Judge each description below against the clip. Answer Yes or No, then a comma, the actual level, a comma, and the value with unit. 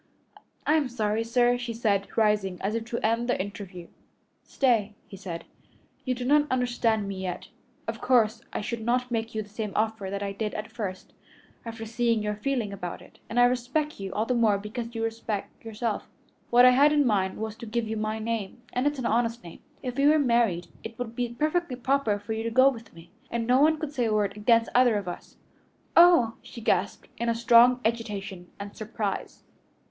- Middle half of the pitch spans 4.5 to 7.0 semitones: No, average, 2.8 semitones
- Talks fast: Yes, fast, 210 wpm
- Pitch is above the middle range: Yes, high, 230 Hz